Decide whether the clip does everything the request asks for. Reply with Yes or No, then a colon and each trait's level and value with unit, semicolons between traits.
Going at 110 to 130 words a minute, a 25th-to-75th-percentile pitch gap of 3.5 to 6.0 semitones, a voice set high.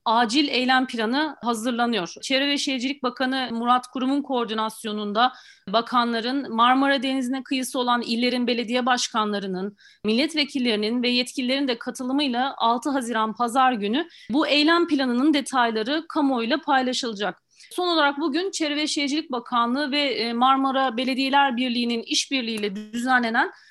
No: average, 120 wpm; average, 2.9 semitones; very high, 255 Hz